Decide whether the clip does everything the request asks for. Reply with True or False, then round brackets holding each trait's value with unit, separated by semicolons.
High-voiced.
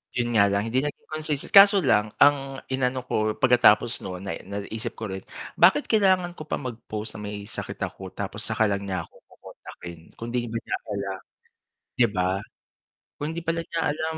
False (120 Hz)